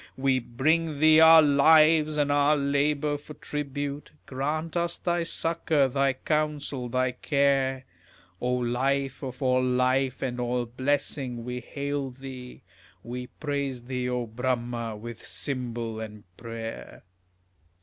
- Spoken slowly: Yes, slow, 130 wpm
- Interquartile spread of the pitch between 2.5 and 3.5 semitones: Yes, average, 2.8 semitones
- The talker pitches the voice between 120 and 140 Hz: Yes, low, 135 Hz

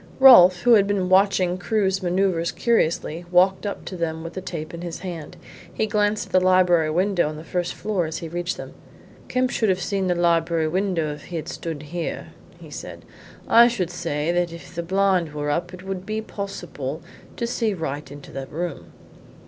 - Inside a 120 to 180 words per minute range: No, average, 200 wpm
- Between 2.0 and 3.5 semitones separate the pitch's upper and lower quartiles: Yes, average, 2.9 semitones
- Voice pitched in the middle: Yes, medium, 175 Hz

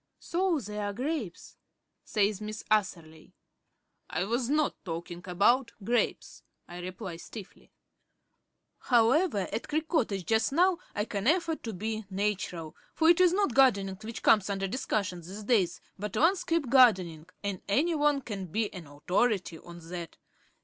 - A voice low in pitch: No, high, 210 Hz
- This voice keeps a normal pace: Yes, average, 150 wpm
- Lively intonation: Yes, wide, 6.3 semitones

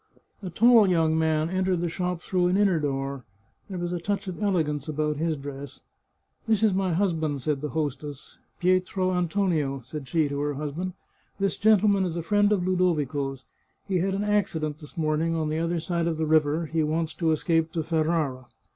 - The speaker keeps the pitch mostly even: No, average, 3.4 semitones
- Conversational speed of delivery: No, fast, 210 wpm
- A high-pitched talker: No, medium, 165 Hz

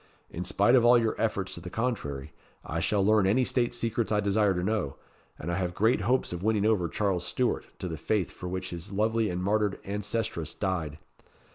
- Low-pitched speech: Yes, low, 100 Hz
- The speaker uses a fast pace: Yes, fast, 210 wpm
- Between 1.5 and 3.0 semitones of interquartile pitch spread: No, average, 3.7 semitones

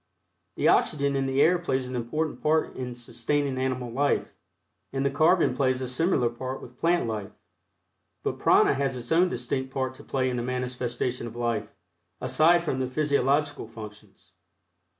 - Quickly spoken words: No, average, 170 wpm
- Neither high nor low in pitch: No, low, 130 Hz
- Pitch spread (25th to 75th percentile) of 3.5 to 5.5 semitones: No, average, 2.8 semitones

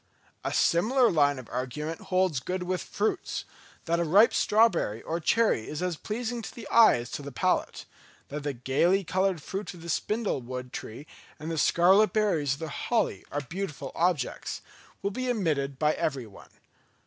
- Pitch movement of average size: No, wide, 5.9 semitones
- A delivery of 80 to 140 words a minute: No, average, 170 wpm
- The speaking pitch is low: No, medium, 170 Hz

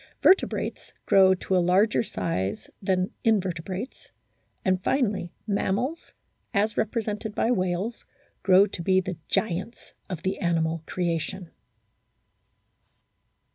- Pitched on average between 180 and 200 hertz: Yes, high, 190 Hz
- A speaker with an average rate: No, slow, 105 wpm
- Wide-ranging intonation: No, average, 3.0 semitones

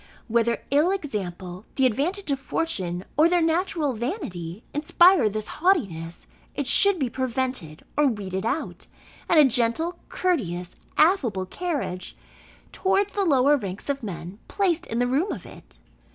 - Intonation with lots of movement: Yes, wide, 8.7 semitones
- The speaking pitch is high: Yes, very high, 265 Hz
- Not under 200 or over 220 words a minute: No, average, 145 wpm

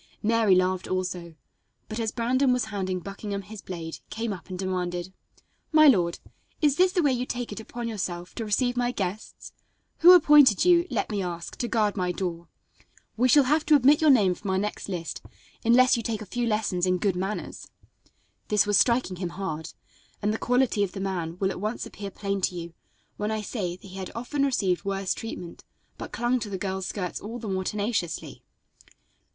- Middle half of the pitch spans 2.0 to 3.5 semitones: No, average, 4.6 semitones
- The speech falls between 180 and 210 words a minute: Yes, average, 200 wpm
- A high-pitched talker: Yes, high, 205 Hz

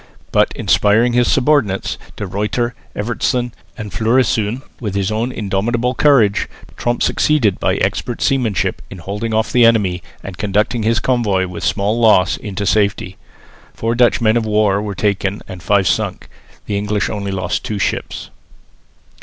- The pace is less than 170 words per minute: Yes, average, 155 wpm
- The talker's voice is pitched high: No, low, 105 Hz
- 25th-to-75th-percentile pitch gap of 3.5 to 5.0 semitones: No, average, 3.1 semitones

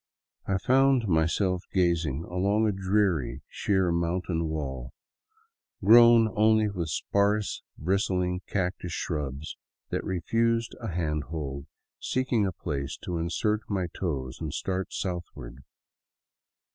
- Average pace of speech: No, slow, 120 wpm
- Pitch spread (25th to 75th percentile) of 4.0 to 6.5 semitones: Yes, average, 4.6 semitones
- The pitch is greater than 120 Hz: No, very low, 90 Hz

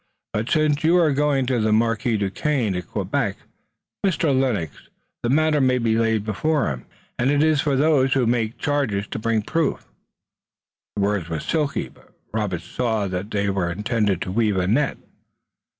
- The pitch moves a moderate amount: No, wide, 5.7 semitones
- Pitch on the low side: Yes, low, 115 Hz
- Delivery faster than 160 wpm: Yes, average, 175 wpm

